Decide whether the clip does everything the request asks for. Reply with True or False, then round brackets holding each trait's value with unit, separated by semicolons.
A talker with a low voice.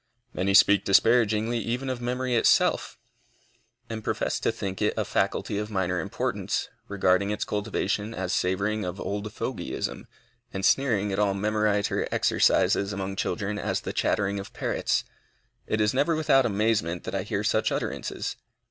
True (105 Hz)